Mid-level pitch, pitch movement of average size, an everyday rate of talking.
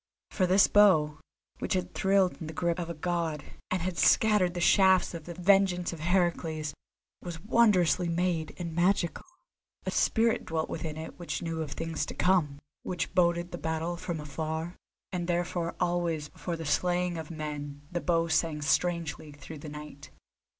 No: medium, 170 Hz; narrow, 2.1 semitones; average, 170 wpm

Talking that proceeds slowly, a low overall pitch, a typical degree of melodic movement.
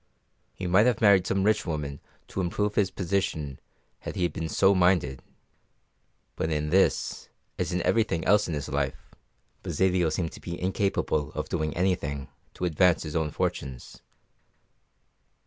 No: average, 150 wpm; very low, 90 Hz; average, 4.0 semitones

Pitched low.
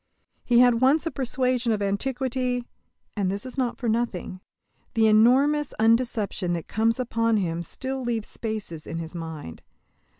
No: high, 230 Hz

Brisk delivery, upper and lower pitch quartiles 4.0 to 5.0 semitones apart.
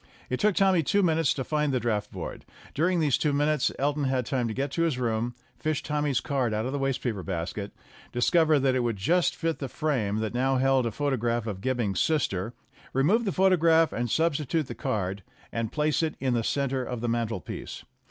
Yes: fast, 210 wpm; average, 4.7 semitones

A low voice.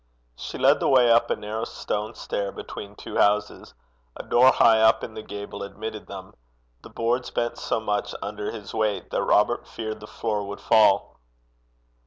Yes: low, 110 Hz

